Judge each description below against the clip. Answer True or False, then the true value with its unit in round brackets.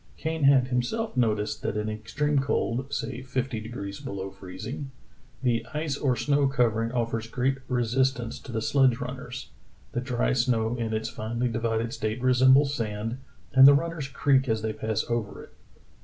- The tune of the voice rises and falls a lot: False (3.1 semitones)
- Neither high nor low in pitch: False (125 Hz)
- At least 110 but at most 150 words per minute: False (165 wpm)